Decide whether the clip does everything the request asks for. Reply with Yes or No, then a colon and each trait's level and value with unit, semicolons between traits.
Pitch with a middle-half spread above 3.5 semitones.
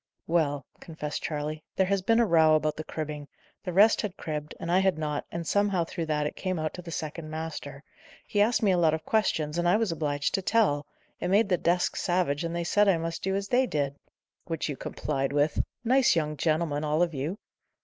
Yes: average, 3.9 semitones